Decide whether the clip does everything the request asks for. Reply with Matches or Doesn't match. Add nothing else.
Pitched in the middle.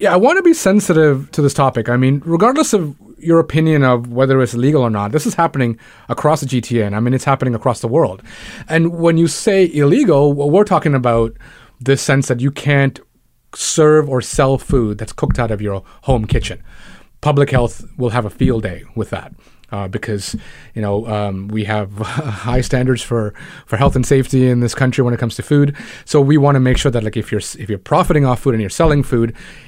Doesn't match